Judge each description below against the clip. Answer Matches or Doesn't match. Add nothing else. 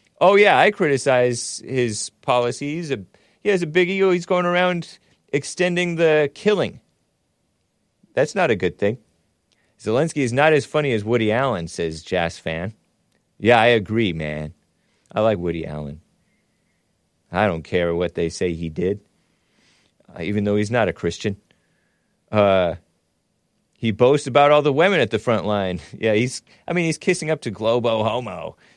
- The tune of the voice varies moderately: Doesn't match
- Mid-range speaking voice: Doesn't match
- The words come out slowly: Doesn't match